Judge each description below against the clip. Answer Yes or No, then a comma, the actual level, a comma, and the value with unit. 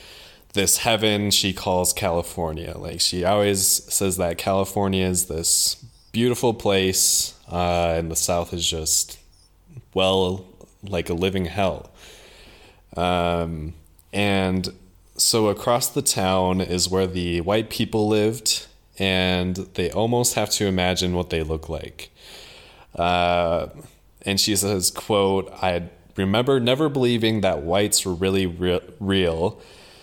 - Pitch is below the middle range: Yes, very low, 95 Hz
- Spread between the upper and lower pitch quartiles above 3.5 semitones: No, average, 2.7 semitones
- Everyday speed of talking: No, slow, 125 wpm